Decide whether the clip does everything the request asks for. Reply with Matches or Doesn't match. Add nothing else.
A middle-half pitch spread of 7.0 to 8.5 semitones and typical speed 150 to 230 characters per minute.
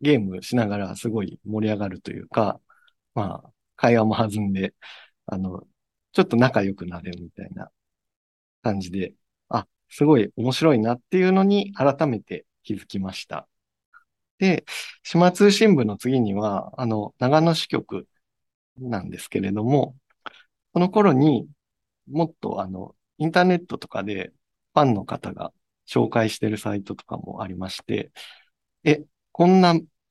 Doesn't match